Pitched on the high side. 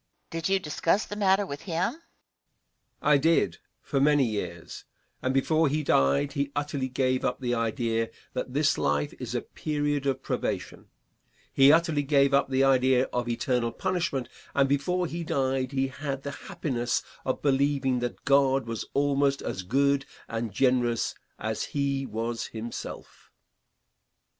No: low, 135 Hz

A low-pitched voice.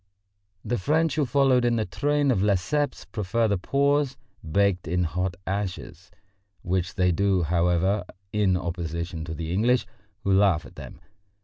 Yes: very low, 95 Hz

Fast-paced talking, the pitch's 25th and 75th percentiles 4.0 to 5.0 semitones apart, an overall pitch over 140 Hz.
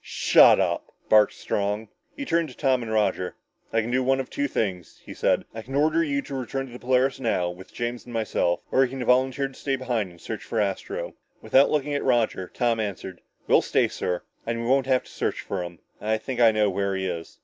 No: fast, 235 wpm; average, 4.5 semitones; low, 120 Hz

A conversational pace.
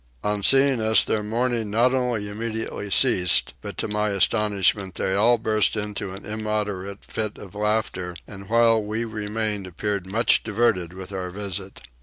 Yes: average, 160 wpm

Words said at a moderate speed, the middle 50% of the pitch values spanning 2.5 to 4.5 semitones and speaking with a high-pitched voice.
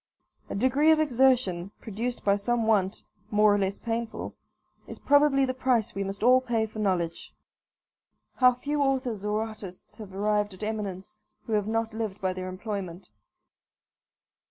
Yes: average, 155 wpm; average, 4.0 semitones; high, 215 Hz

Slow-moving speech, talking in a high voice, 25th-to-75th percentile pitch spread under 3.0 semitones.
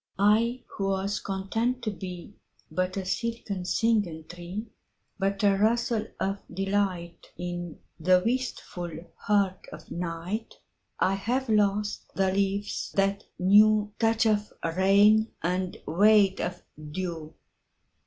Yes: slow, 105 wpm; high, 195 Hz; narrow, 2.6 semitones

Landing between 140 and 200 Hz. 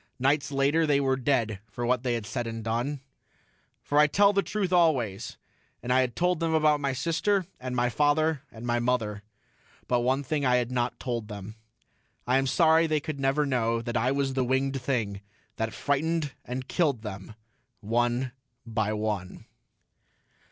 No: low, 130 Hz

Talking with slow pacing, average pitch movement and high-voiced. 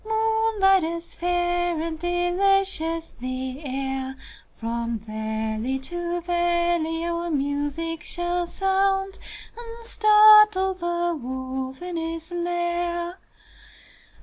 Yes: slow, 95 wpm; average, 4.2 semitones; very high, 345 Hz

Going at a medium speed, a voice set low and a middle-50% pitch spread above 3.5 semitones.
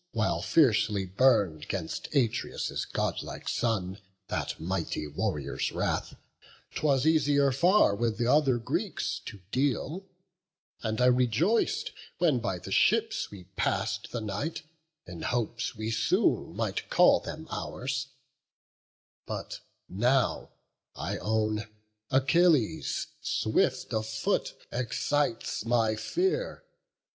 No: slow, 110 wpm; low, 120 Hz; average, 4.8 semitones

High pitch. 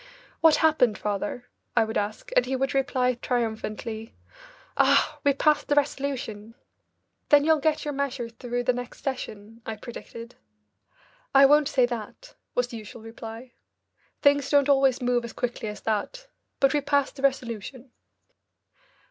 Yes: very high, 250 Hz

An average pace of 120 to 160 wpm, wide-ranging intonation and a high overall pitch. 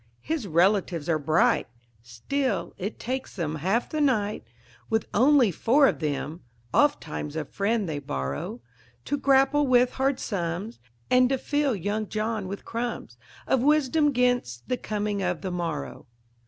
Yes: average, 150 wpm; wide, 7.6 semitones; high, 215 Hz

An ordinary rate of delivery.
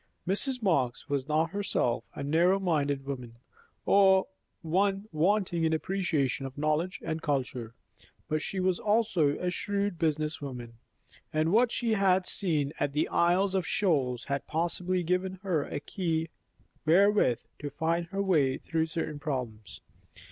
Yes: average, 150 wpm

